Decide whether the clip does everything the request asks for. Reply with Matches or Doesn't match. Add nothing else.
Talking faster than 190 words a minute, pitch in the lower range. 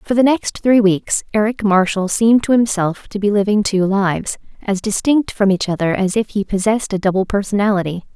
Doesn't match